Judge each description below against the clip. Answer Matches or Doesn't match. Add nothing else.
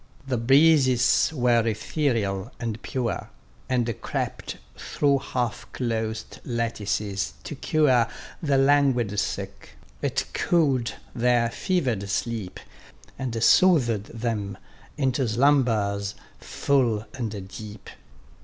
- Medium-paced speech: Doesn't match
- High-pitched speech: Doesn't match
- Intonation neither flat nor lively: Matches